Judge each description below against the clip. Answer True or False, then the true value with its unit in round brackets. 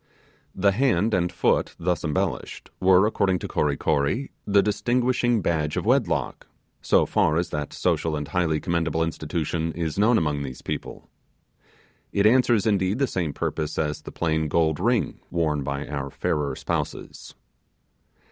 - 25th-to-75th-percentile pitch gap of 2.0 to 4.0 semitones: False (4.9 semitones)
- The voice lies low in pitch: True (85 Hz)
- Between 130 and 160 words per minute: True (150 wpm)